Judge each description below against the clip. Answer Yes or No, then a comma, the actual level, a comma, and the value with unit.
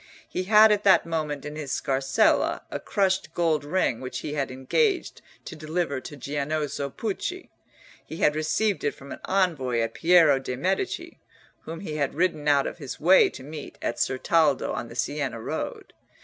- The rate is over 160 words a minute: Yes, average, 175 wpm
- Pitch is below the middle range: No, medium, 150 Hz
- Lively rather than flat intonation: No, average, 4.5 semitones